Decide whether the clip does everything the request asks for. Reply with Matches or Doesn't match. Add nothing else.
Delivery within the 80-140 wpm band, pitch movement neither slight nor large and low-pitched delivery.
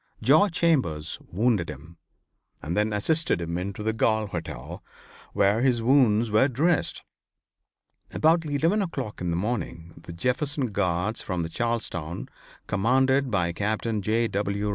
Doesn't match